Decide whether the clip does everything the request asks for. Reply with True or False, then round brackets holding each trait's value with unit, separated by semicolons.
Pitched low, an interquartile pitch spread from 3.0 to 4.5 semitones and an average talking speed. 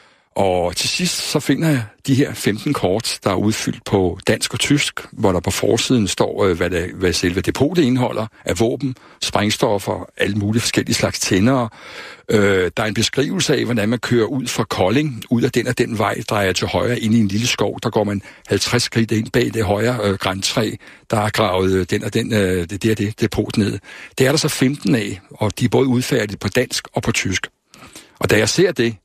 True (110 Hz; 3.5 semitones; 215 wpm)